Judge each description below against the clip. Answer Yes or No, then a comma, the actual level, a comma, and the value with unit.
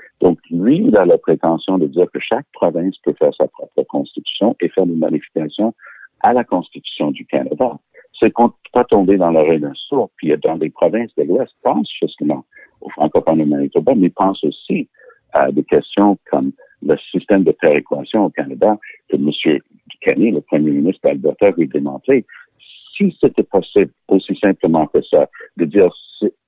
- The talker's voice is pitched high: Yes, very high, 370 Hz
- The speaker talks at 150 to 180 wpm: Yes, average, 175 wpm